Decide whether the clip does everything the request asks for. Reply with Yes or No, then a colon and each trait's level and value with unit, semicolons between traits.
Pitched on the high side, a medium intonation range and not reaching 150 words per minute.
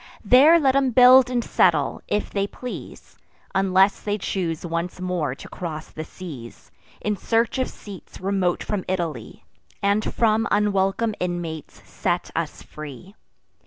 Yes: high, 195 Hz; average, 4.4 semitones; average, 140 wpm